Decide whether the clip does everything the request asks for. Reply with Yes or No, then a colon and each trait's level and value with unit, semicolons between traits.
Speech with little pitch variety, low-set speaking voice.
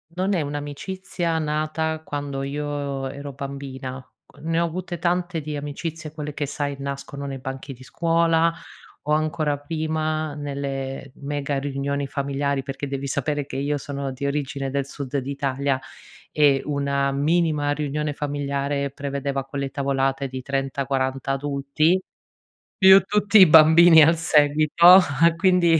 No: narrow, 2.2 semitones; medium, 145 Hz